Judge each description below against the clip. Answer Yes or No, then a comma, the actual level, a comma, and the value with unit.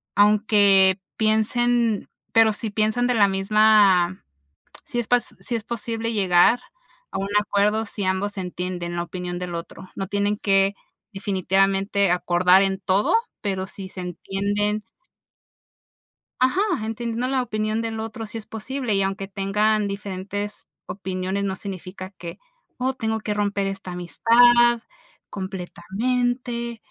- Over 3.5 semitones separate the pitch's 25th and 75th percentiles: No, average, 2.8 semitones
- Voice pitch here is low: No, high, 205 Hz